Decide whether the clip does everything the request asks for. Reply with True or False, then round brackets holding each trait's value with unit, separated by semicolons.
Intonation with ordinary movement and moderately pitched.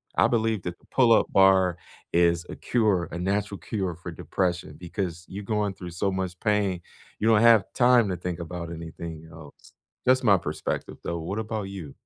False (3.5 semitones; 95 Hz)